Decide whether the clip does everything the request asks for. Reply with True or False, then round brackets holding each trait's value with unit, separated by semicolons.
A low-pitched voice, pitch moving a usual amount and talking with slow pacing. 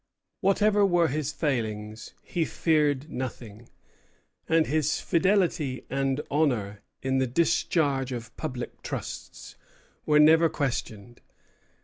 False (145 Hz; 4.6 semitones; 105 wpm)